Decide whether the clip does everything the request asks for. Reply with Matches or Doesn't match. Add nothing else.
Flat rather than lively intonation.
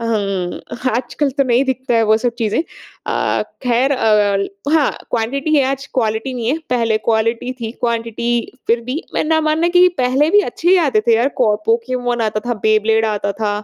Doesn't match